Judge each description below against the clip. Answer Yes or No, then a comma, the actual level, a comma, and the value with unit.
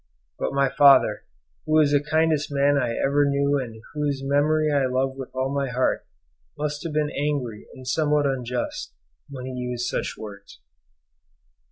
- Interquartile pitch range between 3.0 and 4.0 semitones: No, narrow, 2.4 semitones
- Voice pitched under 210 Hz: Yes, medium, 140 Hz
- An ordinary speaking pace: Yes, average, 165 wpm